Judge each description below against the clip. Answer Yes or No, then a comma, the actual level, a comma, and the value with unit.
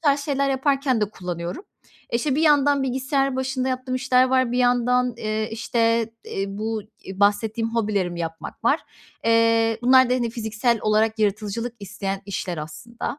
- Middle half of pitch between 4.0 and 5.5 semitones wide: No, average, 3.5 semitones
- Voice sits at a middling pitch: No, high, 230 Hz